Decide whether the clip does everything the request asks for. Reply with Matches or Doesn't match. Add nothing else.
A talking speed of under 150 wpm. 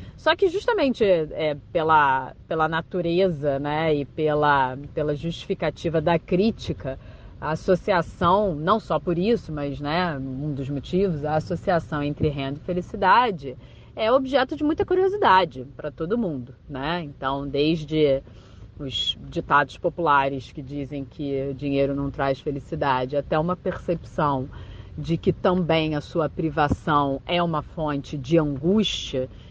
Matches